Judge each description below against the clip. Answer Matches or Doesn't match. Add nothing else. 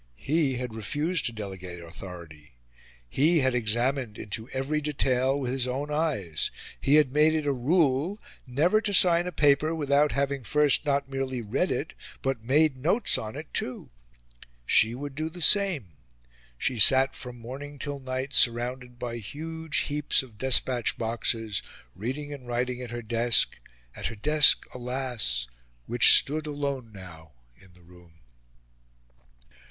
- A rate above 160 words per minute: Doesn't match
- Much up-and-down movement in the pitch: Doesn't match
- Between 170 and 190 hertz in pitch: Doesn't match